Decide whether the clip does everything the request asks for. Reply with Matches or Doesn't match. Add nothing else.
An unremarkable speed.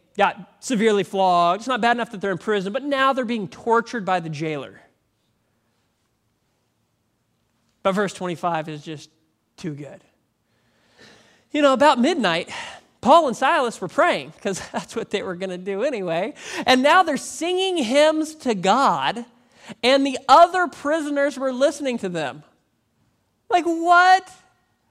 Matches